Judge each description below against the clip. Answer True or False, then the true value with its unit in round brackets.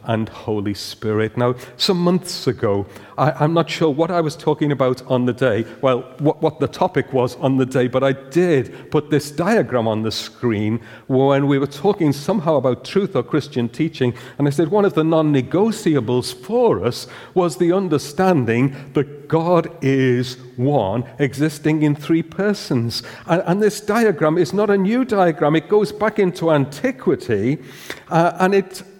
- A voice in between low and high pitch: True (150 Hz)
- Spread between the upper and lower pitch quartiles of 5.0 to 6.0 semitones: True (5.6 semitones)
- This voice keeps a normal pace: True (175 wpm)